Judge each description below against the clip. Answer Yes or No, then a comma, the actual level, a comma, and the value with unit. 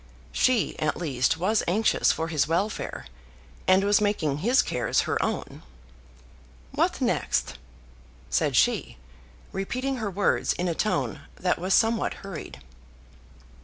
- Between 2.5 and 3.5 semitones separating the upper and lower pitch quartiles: No, average, 4.8 semitones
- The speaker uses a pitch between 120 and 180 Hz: No, high, 190 Hz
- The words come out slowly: Yes, slow, 130 wpm